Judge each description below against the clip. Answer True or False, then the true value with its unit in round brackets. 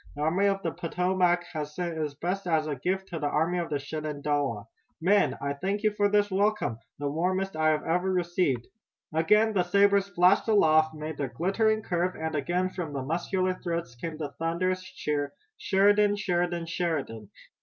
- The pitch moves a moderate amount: True (3.7 semitones)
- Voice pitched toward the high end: False (175 Hz)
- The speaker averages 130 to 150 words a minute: False (175 wpm)